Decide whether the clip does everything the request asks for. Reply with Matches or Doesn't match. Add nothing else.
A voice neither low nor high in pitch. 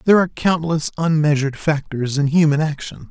Matches